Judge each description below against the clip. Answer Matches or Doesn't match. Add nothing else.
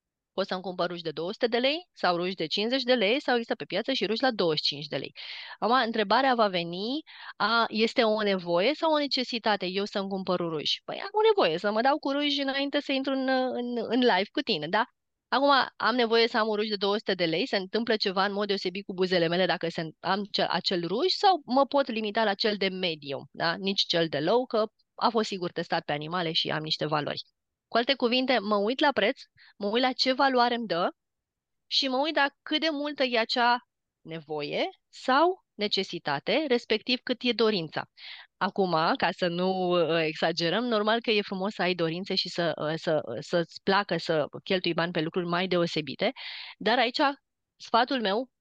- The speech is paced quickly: Matches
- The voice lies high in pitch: Matches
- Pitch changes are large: Matches